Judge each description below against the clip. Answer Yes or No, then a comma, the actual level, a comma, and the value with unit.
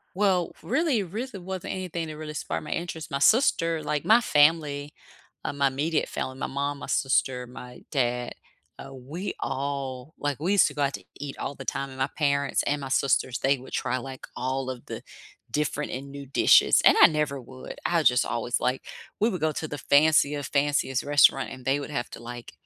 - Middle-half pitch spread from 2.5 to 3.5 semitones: Yes, average, 3.0 semitones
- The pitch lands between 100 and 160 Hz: Yes, medium, 140 Hz